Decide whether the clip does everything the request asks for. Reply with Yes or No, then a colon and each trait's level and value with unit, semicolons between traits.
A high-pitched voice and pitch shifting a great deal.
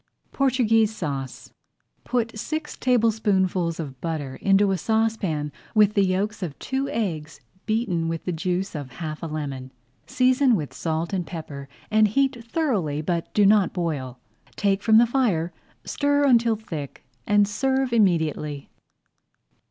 Yes: high, 195 Hz; wide, 6.1 semitones